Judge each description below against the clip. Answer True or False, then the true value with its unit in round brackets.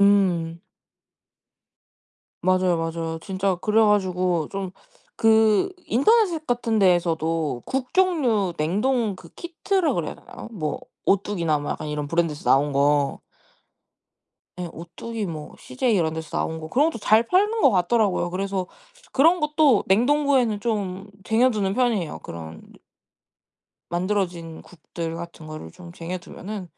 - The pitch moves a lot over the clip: True (5.7 semitones)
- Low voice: False (190 Hz)